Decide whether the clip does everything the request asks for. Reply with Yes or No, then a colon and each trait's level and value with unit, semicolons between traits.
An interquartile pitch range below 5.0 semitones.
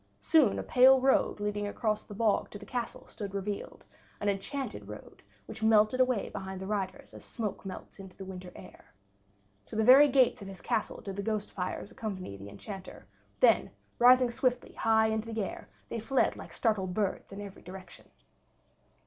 Yes: average, 3.5 semitones